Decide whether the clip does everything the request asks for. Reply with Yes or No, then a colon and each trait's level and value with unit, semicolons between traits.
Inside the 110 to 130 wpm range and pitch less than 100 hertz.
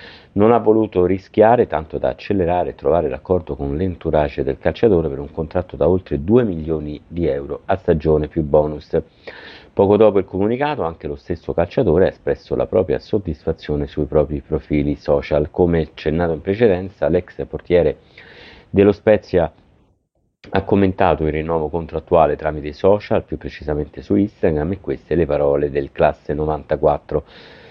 No: average, 155 wpm; very low, 80 Hz